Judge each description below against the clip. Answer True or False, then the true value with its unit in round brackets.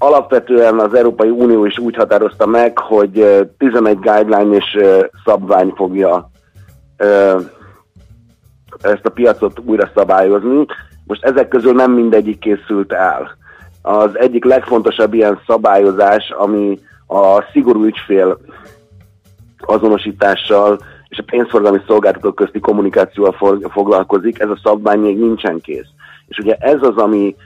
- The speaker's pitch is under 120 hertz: True (105 Hz)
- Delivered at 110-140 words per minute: True (120 wpm)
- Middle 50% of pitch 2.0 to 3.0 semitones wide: True (2.7 semitones)